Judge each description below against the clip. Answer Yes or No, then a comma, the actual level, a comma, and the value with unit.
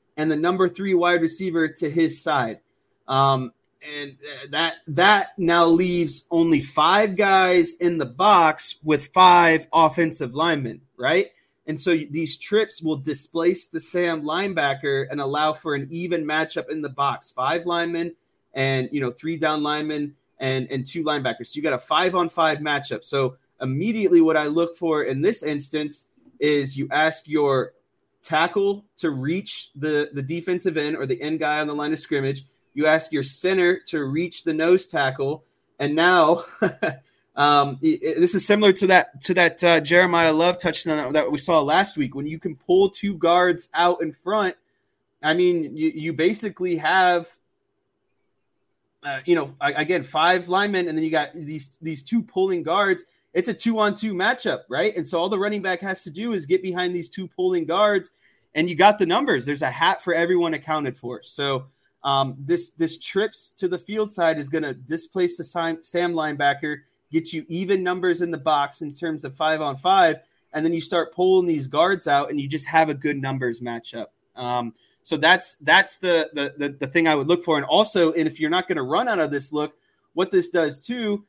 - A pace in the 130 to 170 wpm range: No, average, 190 wpm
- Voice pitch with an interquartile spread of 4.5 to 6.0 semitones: No, average, 3.4 semitones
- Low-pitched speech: No, medium, 165 Hz